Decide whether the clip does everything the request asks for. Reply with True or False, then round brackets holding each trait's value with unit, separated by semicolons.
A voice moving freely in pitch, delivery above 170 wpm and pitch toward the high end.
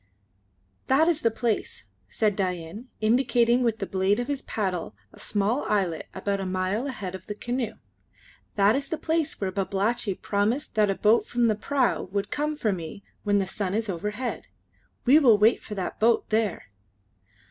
False (3.7 semitones; 180 wpm; 210 Hz)